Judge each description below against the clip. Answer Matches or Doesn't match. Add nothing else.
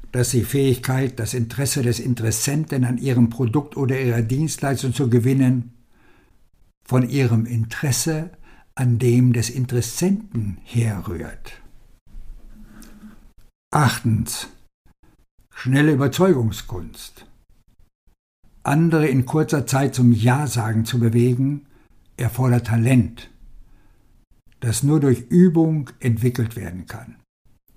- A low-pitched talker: Matches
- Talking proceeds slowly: Matches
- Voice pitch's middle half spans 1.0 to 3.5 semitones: Matches